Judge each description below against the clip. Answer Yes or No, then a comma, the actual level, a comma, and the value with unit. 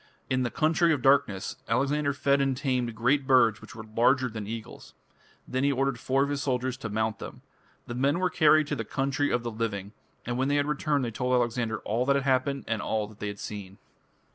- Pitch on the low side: Yes, low, 130 Hz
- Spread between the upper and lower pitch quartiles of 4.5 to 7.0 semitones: No, average, 3.6 semitones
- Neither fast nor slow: No, fast, 220 wpm